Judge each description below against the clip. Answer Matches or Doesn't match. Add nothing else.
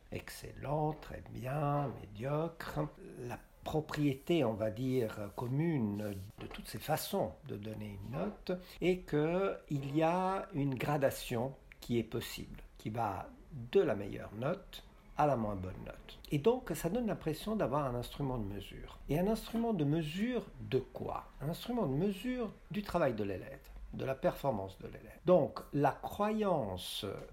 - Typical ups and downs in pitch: Doesn't match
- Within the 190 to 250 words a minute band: Doesn't match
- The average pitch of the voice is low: Doesn't match